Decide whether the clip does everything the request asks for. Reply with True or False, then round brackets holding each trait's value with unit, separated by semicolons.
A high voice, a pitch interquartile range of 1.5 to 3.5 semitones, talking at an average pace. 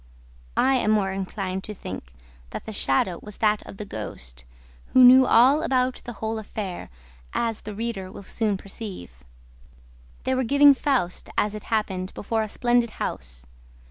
False (215 Hz; 4.2 semitones; 165 wpm)